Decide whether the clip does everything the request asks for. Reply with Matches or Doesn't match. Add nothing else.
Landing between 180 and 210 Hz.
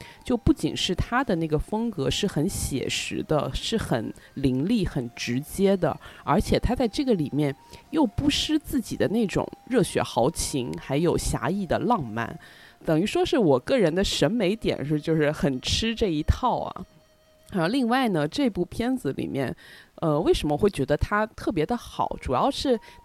Matches